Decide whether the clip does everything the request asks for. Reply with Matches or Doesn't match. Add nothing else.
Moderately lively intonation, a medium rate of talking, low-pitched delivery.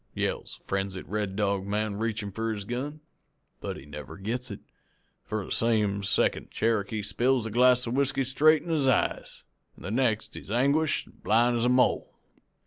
Matches